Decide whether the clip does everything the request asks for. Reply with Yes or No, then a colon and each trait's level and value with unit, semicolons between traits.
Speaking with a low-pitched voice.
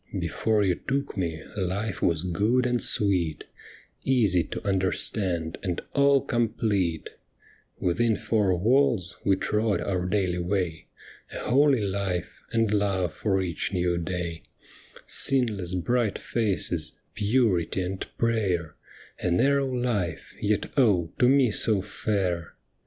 Yes: low, 100 Hz